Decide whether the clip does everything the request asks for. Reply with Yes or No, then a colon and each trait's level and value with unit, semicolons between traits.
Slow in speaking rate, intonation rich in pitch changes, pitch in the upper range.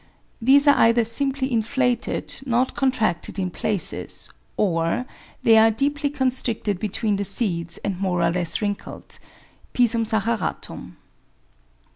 No: slow, 120 wpm; average, 4.5 semitones; high, 225 Hz